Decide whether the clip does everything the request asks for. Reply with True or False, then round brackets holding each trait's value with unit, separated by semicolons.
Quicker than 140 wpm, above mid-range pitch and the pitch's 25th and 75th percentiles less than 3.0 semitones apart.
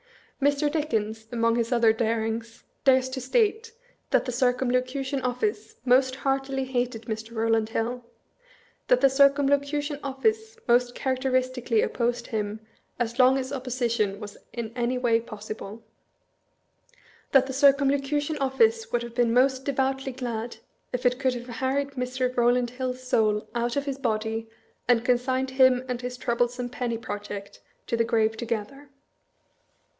True (150 wpm; 250 Hz; 2.5 semitones)